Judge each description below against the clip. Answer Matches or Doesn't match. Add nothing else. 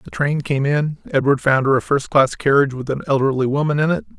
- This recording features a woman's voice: Doesn't match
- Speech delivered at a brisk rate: Matches